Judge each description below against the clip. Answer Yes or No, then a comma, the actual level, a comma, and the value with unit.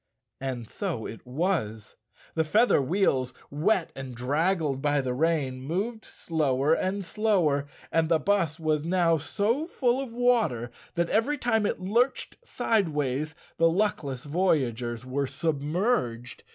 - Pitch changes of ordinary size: No, wide, 7.0 semitones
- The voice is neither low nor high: Yes, medium, 160 Hz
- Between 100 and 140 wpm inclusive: Yes, slow, 135 wpm